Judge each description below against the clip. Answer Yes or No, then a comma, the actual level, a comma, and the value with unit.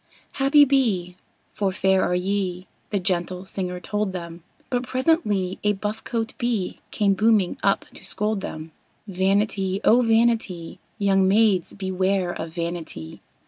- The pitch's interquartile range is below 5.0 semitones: Yes, average, 3.2 semitones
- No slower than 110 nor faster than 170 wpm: Yes, average, 140 wpm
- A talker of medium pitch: No, high, 195 Hz